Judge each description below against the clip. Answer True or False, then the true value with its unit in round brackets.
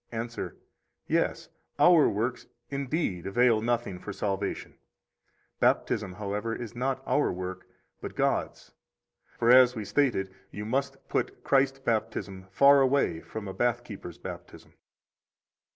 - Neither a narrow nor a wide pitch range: True (4.8 semitones)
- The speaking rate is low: True (125 wpm)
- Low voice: True (115 Hz)